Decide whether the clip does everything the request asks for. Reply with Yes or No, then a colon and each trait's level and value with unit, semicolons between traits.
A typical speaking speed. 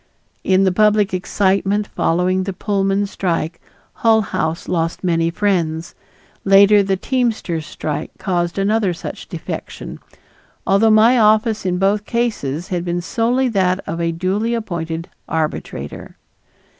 No: slow, 130 wpm